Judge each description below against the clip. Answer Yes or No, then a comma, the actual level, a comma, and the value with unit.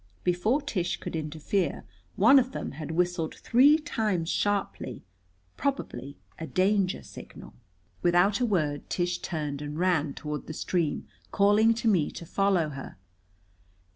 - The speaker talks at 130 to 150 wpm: Yes, average, 140 wpm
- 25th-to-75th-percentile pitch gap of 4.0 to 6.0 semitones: Yes, average, 4.8 semitones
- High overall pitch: No, medium, 180 Hz